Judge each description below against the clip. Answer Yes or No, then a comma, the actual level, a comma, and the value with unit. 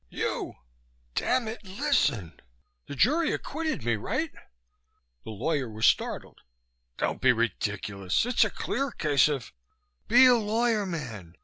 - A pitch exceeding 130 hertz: Yes, high, 190 Hz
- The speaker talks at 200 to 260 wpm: No, slow, 135 wpm